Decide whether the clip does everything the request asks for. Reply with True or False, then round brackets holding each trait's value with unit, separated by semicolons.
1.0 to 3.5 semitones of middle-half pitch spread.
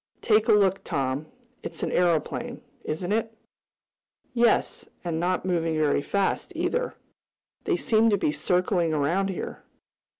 False (4.9 semitones)